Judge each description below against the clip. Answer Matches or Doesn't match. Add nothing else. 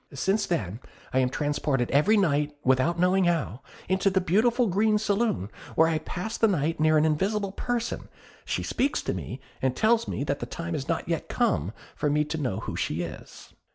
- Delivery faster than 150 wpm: Matches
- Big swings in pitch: Matches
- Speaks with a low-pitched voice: Doesn't match